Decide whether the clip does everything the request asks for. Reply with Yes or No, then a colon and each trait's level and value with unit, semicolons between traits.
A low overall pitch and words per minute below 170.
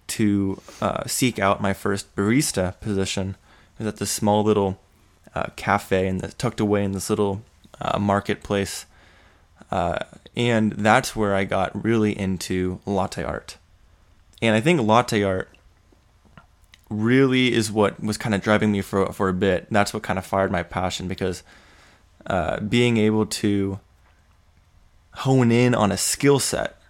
Yes: low, 100 Hz; average, 155 wpm